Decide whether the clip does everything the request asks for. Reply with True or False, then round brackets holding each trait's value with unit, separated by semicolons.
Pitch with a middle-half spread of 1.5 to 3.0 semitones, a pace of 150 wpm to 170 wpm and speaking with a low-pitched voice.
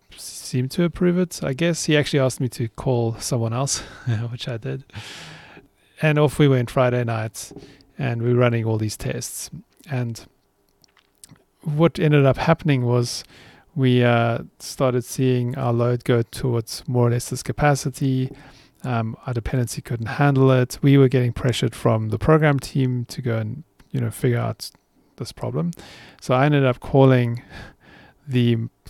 True (2.7 semitones; 160 wpm; 130 Hz)